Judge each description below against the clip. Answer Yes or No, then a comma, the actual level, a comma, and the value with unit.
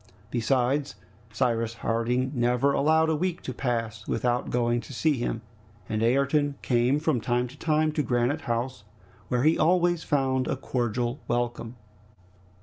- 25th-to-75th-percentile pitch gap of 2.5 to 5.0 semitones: Yes, average, 3.4 semitones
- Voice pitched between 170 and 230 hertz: No, low, 125 Hz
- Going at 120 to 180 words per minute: Yes, average, 145 wpm